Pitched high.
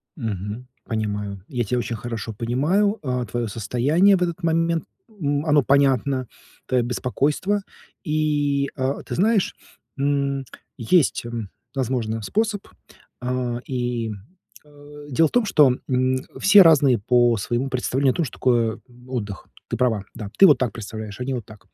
No: low, 130 Hz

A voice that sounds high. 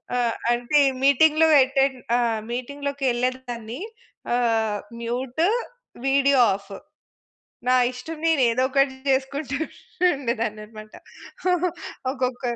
Yes: very high, 260 Hz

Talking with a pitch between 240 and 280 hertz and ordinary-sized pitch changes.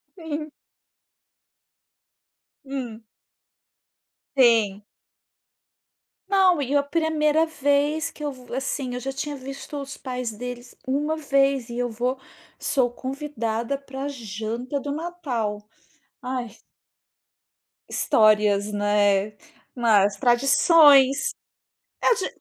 Yes: very high, 265 Hz; average, 4.1 semitones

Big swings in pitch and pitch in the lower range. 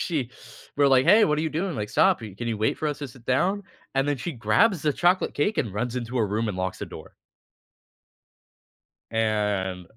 Yes: wide, 6.0 semitones; low, 125 Hz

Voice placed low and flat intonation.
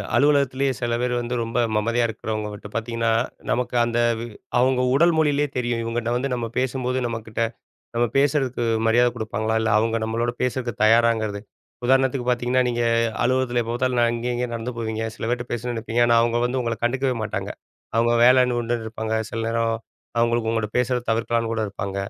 Yes: low, 120 Hz; narrow, 1.7 semitones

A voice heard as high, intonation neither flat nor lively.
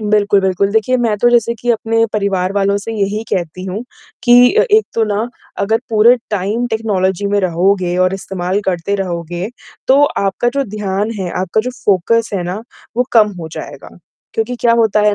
Yes: high, 205 Hz; average, 3.1 semitones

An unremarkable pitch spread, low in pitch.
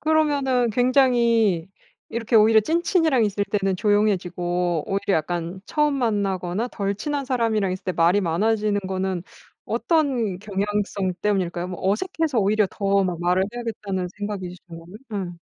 No: average, 4.1 semitones; high, 205 Hz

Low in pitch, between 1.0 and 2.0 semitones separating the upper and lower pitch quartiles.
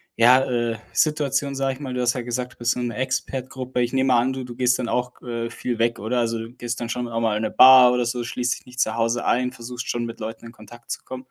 Yes: low, 125 Hz; narrow, 1.5 semitones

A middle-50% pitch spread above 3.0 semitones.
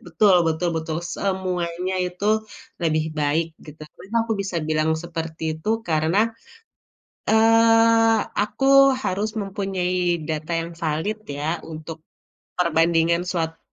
Yes: average, 3.8 semitones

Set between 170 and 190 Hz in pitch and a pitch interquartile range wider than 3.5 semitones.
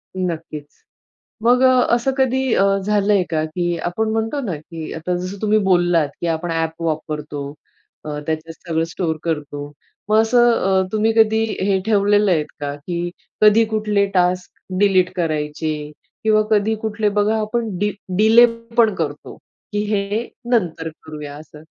Yes: medium, 185 Hz; average, 5.2 semitones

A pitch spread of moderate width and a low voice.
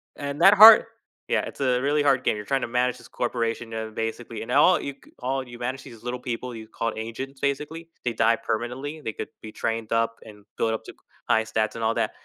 Yes: average, 3.3 semitones; low, 120 Hz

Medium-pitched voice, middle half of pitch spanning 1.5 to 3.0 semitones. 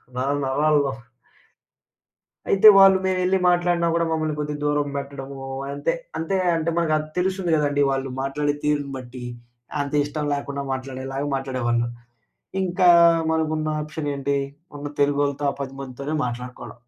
Yes: medium, 145 Hz; narrow, 2.5 semitones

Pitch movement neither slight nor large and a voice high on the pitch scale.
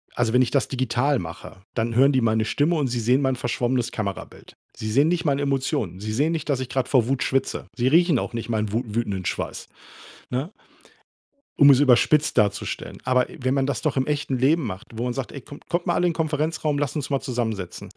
No: average, 3.6 semitones; low, 130 Hz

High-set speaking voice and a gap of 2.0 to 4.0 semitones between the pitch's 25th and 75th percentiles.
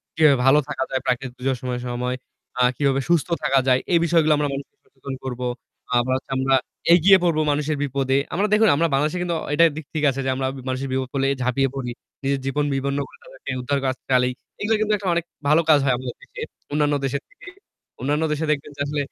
No: medium, 140 Hz; average, 2.9 semitones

